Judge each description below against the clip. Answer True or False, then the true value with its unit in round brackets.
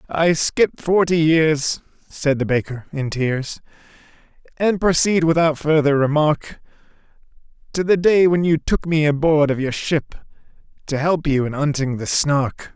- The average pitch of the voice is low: False (155 Hz)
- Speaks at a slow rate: False (150 wpm)